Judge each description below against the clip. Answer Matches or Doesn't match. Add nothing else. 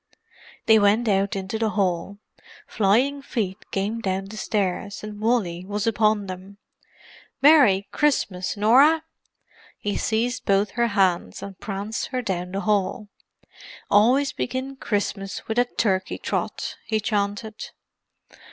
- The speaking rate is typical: Doesn't match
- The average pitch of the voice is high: Matches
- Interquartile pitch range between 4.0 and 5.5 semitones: Doesn't match